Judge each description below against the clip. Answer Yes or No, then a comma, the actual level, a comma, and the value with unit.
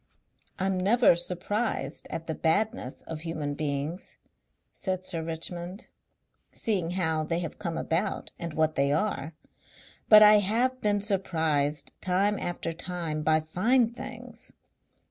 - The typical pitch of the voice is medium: Yes, medium, 175 Hz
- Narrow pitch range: No, average, 4.6 semitones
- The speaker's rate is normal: No, slow, 130 wpm